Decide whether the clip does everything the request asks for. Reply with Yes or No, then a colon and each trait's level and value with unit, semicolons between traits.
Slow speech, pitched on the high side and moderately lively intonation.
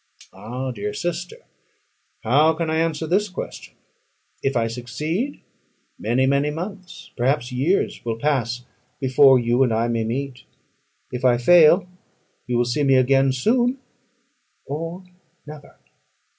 No: slow, 130 wpm; low, 135 Hz; average, 4.9 semitones